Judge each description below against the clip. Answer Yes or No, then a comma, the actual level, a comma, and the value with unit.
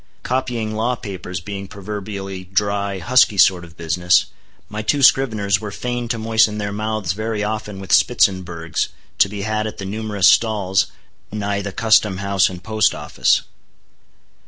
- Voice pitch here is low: Yes, low, 105 Hz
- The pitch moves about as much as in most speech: No, narrow, 2.3 semitones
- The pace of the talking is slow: No, average, 155 wpm